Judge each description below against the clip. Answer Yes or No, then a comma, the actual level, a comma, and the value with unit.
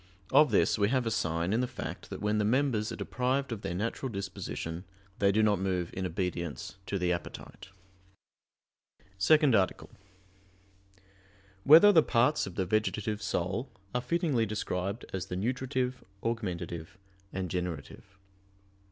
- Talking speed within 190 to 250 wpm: No, average, 165 wpm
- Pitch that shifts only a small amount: No, average, 5.1 semitones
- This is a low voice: Yes, low, 100 Hz